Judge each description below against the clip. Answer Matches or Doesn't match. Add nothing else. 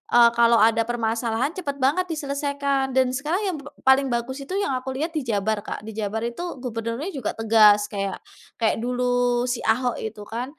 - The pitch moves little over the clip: Doesn't match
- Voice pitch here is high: Matches